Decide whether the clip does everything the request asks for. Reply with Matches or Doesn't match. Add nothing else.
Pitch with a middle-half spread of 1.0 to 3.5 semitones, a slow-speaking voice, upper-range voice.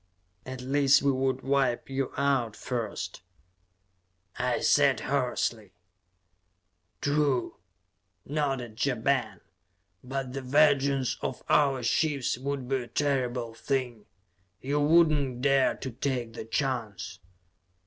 Doesn't match